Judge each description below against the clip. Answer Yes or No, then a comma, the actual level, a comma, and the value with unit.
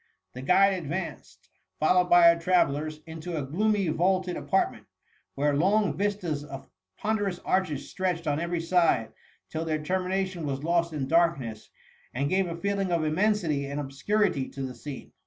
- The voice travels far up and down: No, average, 4.3 semitones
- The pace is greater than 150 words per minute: Yes, average, 175 wpm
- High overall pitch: No, medium, 170 Hz